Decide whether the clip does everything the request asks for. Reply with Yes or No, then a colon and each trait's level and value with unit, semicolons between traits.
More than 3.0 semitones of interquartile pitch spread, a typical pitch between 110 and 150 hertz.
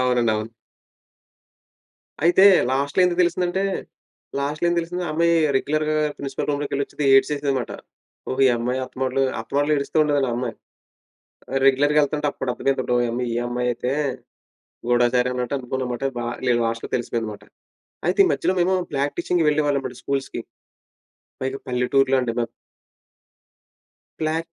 Yes: average, 3.4 semitones; low, 135 Hz